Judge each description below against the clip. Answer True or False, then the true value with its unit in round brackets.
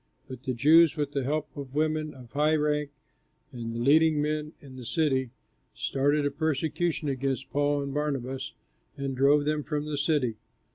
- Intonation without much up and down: True (2.2 semitones)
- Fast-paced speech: False (175 wpm)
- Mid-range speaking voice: True (145 Hz)